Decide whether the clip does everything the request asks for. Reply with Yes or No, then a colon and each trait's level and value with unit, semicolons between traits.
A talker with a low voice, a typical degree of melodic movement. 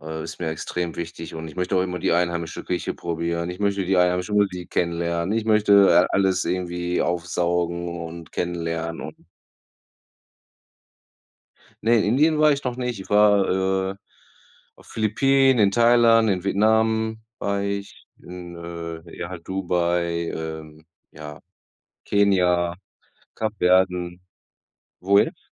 Yes: very low, 90 Hz; average, 3.1 semitones